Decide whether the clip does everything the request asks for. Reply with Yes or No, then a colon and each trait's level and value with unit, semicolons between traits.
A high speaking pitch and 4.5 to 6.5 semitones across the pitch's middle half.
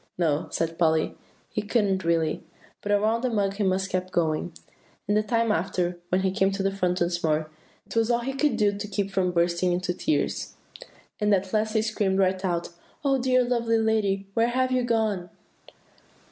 No: high, 195 Hz; average, 3.7 semitones